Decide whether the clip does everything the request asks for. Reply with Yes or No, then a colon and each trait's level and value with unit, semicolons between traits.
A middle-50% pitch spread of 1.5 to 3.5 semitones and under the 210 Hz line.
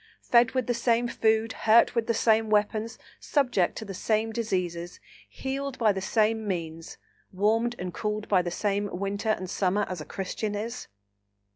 No: average, 3.1 semitones; high, 215 Hz